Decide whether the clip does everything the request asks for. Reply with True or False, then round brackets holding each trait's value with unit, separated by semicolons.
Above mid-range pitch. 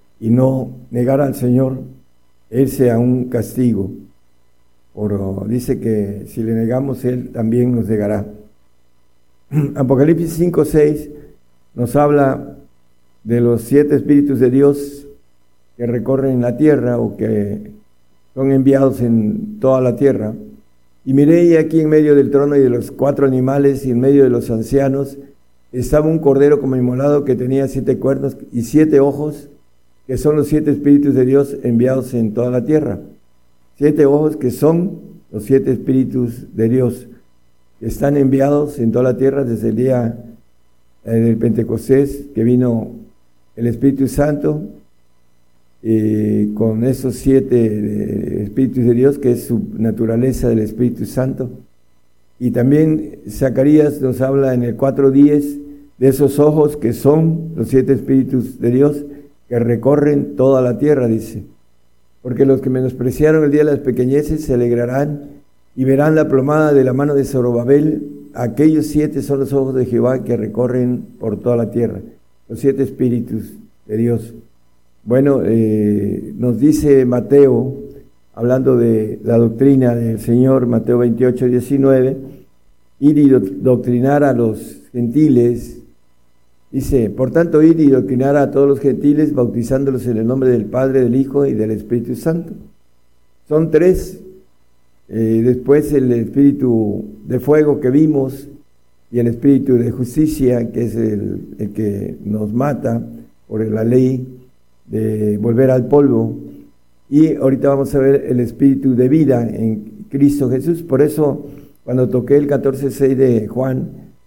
False (125 Hz)